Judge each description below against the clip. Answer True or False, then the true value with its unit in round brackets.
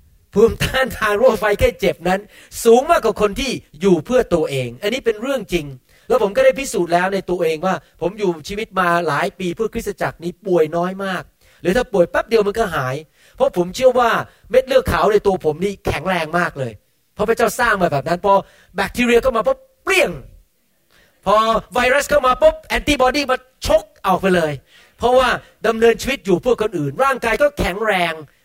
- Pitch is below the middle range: False (205 Hz)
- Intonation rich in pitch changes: True (6.2 semitones)